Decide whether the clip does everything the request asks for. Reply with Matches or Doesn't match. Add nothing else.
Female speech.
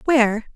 Matches